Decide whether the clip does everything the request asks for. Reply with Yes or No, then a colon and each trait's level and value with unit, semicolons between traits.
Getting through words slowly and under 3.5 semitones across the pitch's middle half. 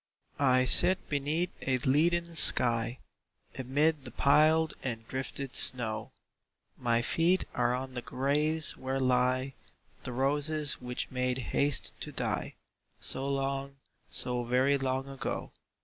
Yes: slow, 130 wpm; narrow, 2.6 semitones